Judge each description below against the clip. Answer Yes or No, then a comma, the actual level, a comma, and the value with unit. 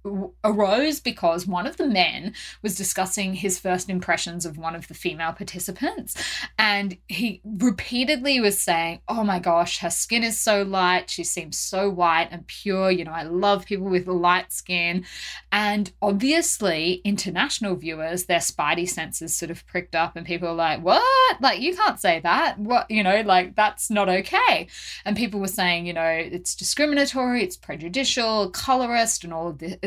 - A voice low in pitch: No, high, 190 Hz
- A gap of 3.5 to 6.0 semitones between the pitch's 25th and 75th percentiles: Yes, average, 4.0 semitones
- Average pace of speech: Yes, average, 175 wpm